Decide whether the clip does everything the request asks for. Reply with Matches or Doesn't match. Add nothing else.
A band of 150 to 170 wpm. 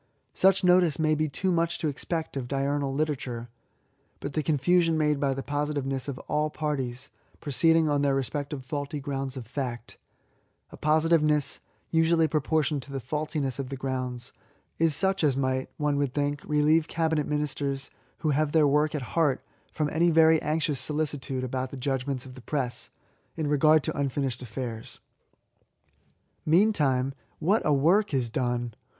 Matches